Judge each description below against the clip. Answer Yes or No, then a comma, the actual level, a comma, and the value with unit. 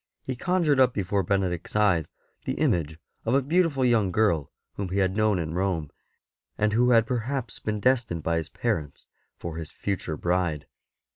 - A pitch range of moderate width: No, wide, 6.2 semitones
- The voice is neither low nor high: No, low, 100 Hz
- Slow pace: No, average, 170 wpm